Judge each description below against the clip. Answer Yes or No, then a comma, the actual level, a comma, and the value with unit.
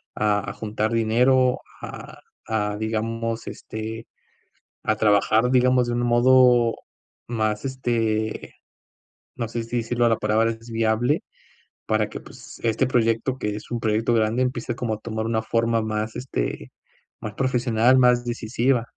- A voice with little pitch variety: Yes, narrow, 1.8 semitones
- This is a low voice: Yes, low, 115 Hz